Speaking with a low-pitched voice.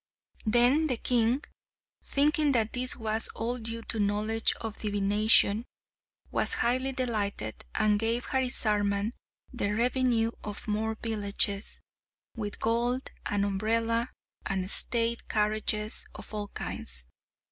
No: high, 225 Hz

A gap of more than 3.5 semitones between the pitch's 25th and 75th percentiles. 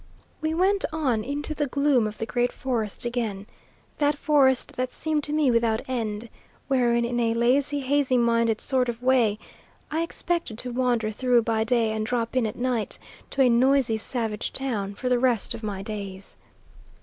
No: average, 3.2 semitones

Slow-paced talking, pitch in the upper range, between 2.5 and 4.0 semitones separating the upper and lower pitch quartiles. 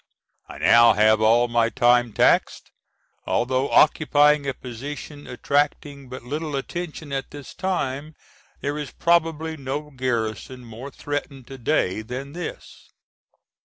No: slow, 130 wpm; low, 135 Hz; average, 3.5 semitones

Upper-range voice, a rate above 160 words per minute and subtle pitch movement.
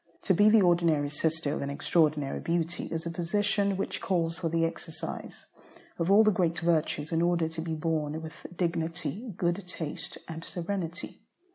No: medium, 165 Hz; average, 170 wpm; narrow, 1.8 semitones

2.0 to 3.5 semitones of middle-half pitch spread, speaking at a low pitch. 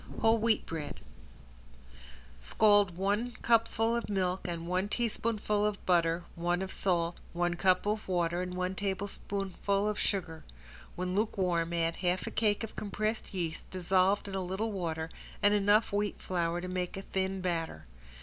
No: average, 2.9 semitones; high, 190 Hz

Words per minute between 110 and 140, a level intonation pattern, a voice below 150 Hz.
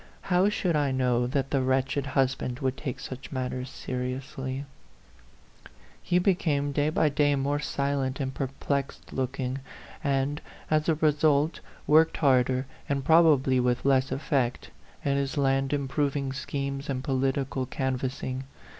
Yes: slow, 135 wpm; narrow, 1.7 semitones; low, 135 Hz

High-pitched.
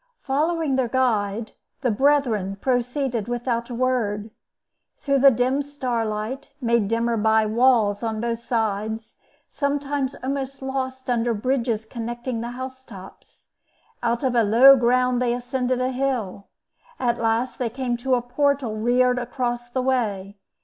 Yes: high, 245 Hz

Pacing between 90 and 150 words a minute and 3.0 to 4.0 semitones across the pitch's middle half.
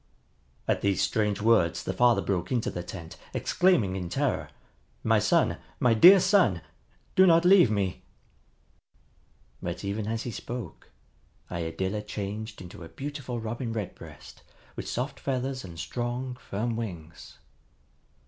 No: slow, 135 wpm; average, 4.9 semitones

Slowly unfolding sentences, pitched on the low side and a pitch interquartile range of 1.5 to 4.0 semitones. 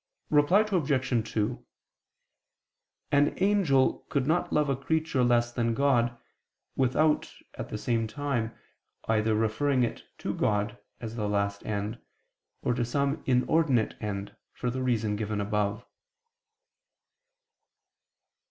No: slow, 120 wpm; low, 120 Hz; average, 4.6 semitones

